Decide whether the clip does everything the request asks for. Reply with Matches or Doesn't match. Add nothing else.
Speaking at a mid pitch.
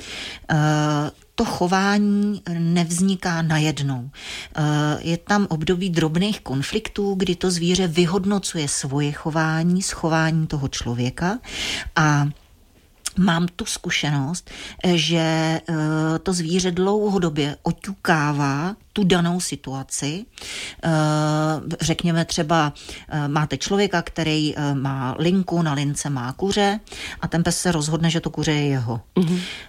Matches